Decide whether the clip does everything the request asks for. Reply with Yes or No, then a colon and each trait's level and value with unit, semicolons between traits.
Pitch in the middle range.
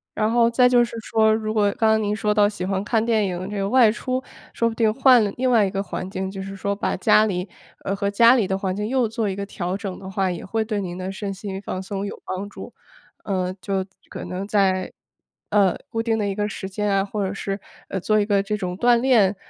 No: high, 205 Hz